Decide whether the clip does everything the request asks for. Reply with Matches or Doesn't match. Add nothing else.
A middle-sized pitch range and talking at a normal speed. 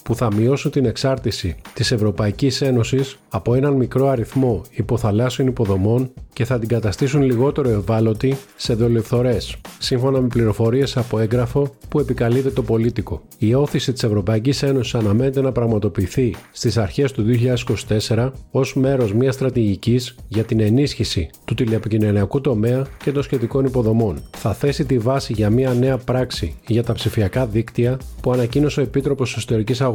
Matches